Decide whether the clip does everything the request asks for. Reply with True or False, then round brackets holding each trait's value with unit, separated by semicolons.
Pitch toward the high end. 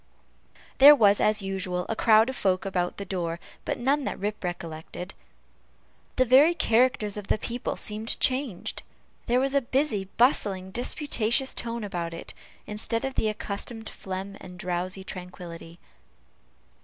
True (210 Hz)